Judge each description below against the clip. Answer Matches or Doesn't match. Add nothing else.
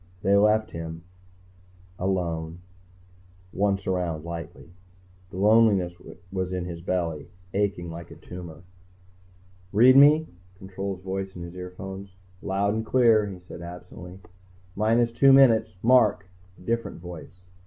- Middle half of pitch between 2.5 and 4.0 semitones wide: Matches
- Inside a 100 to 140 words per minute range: Matches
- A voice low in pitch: Matches